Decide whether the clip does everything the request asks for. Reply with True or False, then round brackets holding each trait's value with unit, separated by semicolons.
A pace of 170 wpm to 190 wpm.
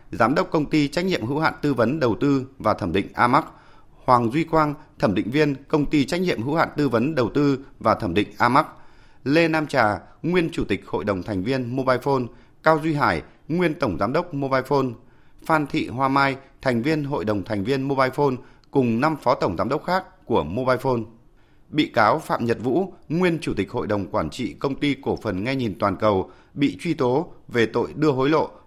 False (225 wpm)